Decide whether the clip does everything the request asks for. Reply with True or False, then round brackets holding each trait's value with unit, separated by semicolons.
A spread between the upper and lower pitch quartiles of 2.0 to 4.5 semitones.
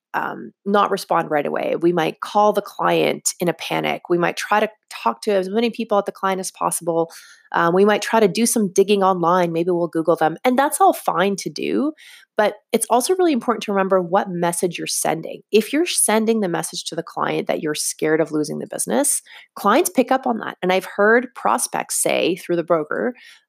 False (5.1 semitones)